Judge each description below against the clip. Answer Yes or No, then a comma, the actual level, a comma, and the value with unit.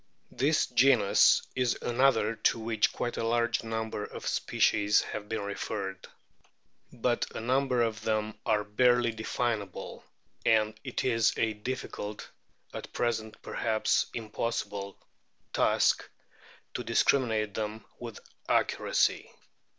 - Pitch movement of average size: No, narrow, 2.1 semitones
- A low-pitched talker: Yes, low, 110 Hz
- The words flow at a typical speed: No, slow, 115 wpm